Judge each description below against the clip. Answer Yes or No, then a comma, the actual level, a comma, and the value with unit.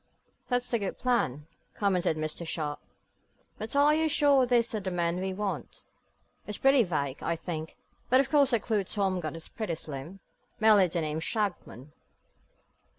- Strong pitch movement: Yes, wide, 6.5 semitones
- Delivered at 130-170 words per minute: Yes, average, 165 wpm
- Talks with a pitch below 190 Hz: No, high, 195 Hz